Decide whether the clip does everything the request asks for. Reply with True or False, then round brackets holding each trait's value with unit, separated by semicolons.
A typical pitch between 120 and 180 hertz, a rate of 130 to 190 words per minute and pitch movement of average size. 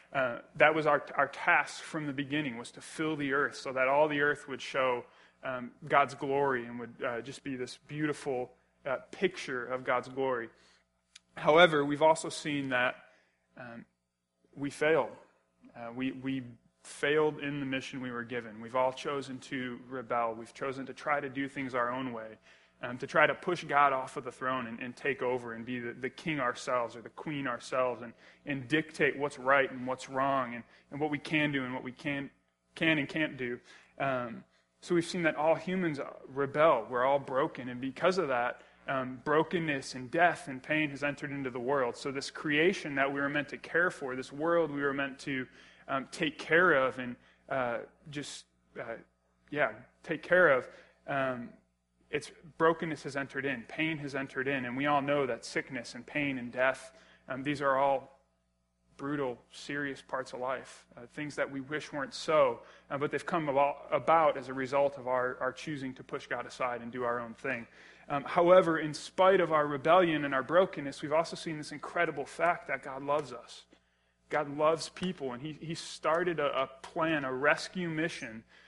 False (140 Hz; 200 wpm; 3.1 semitones)